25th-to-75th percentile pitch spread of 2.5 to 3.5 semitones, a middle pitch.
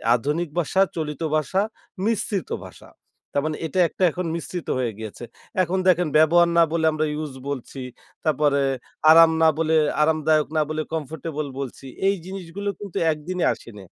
Yes: average, 2.8 semitones; medium, 160 Hz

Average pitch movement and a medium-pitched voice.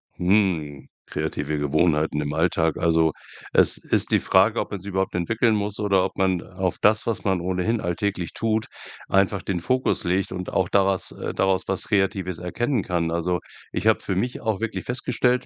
No: average, 3.1 semitones; very low, 95 Hz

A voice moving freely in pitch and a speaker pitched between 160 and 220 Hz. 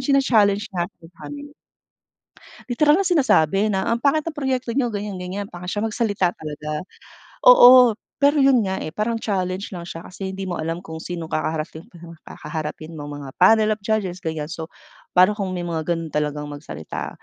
Yes: wide, 5.9 semitones; high, 190 Hz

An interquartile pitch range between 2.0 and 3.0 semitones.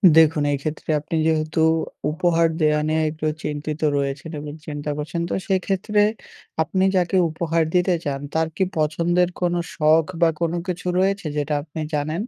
Yes: narrow, 2.5 semitones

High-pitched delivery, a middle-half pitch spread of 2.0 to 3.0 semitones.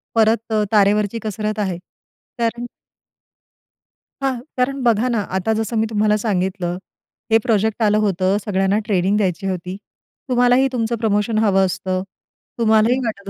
Yes: high, 210 Hz; narrow, 2.6 semitones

